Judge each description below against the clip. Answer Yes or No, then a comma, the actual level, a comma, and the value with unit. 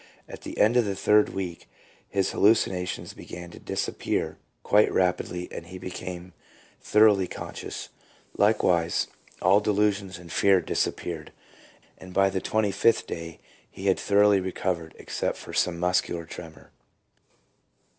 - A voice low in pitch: Yes, very low, 95 Hz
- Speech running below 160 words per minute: Yes, slow, 135 wpm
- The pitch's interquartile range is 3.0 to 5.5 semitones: No, narrow, 2.6 semitones